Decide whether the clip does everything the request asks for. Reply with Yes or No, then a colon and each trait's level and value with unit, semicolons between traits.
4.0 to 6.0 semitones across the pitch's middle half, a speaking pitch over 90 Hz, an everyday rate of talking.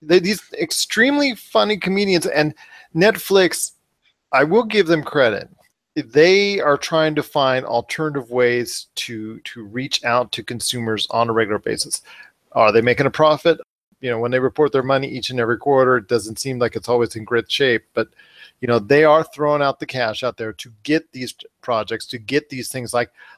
Yes: average, 5.1 semitones; low, 135 Hz; average, 185 wpm